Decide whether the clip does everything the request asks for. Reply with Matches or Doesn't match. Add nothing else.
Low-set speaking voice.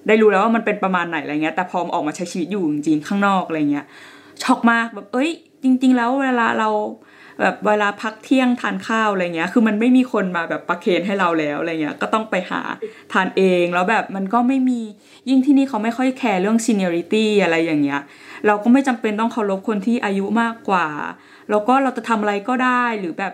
Doesn't match